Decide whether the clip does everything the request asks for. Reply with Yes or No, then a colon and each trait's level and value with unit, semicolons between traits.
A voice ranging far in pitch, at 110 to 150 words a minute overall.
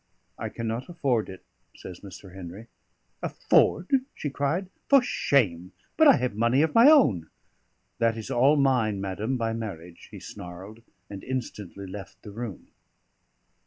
Yes: wide, 6.1 semitones; average, 145 wpm